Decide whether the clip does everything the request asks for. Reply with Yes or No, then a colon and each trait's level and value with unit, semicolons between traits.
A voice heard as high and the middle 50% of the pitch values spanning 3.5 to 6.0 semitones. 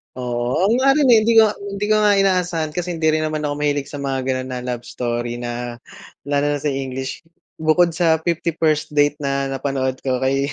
No: medium, 145 Hz; average, 4.6 semitones